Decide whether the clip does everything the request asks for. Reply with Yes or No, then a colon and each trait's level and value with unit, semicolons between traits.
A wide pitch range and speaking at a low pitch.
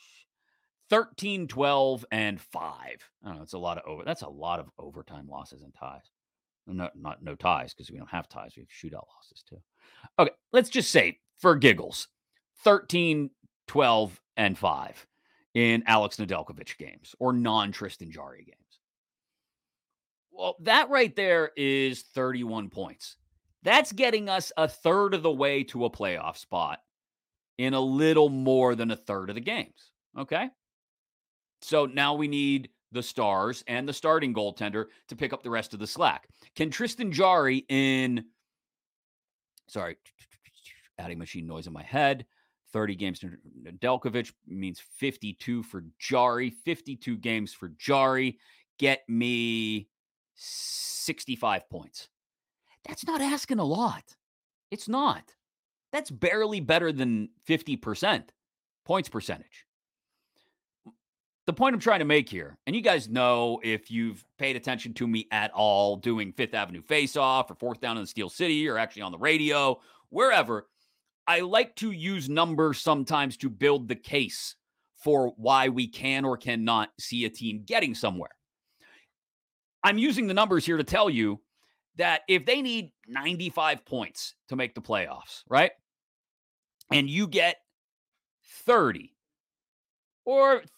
Yes: wide, 6.4 semitones; low, 130 Hz